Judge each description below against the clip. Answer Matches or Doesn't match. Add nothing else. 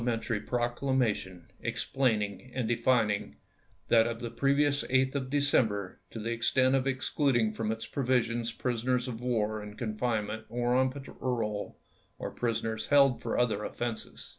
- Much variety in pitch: Doesn't match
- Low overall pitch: Matches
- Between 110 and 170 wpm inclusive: Matches